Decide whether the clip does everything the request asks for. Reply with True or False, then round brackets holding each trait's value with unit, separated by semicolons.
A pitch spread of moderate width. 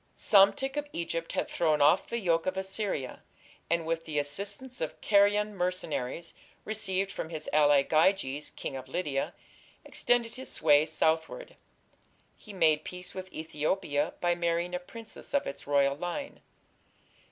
True (4.6 semitones)